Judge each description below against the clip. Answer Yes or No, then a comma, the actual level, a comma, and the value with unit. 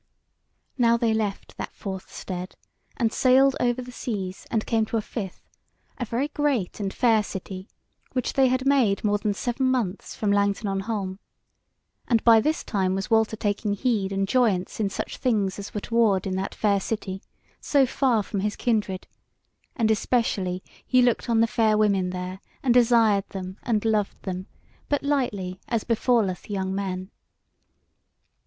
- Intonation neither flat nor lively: Yes, average, 3.5 semitones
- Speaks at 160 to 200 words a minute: Yes, average, 170 wpm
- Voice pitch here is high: Yes, high, 215 Hz